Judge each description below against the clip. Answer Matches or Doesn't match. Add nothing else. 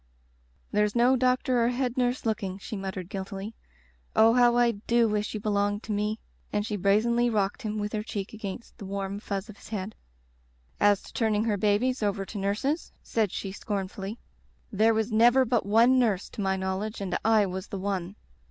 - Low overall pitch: Doesn't match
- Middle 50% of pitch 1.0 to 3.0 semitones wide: Matches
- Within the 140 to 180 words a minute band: Doesn't match